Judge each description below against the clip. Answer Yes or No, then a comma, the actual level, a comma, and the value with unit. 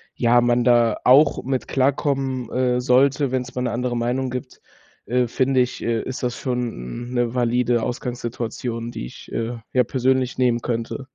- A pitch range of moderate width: No, narrow, 1.4 semitones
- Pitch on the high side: No, low, 125 Hz